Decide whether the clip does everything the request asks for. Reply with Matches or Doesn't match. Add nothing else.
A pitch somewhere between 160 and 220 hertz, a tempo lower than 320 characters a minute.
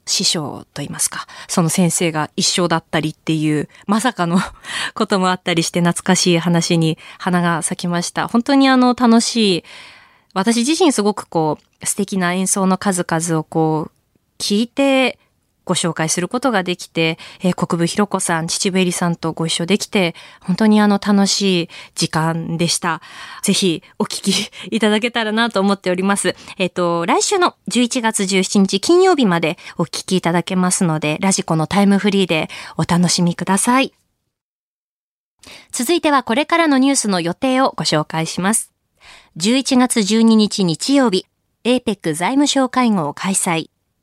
Matches